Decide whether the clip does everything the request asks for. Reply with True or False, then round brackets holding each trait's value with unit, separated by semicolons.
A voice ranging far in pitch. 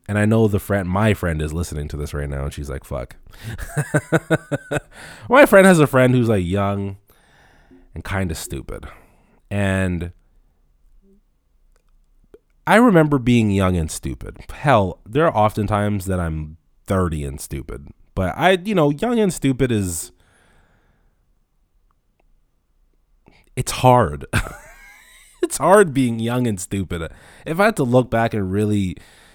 True (7.5 semitones)